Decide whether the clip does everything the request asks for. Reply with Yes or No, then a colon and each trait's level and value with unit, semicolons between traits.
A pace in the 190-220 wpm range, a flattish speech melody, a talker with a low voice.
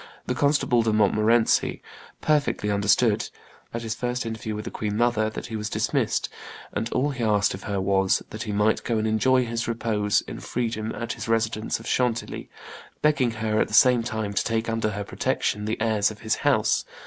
Yes: average, 195 wpm; narrow, 1.8 semitones; low, 110 Hz